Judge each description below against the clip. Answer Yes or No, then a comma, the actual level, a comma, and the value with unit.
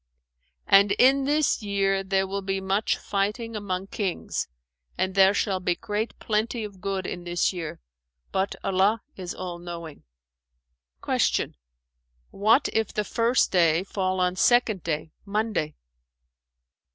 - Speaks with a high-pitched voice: Yes, high, 195 Hz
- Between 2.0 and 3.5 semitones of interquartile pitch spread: Yes, narrow, 2.5 semitones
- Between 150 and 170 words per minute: No, average, 140 wpm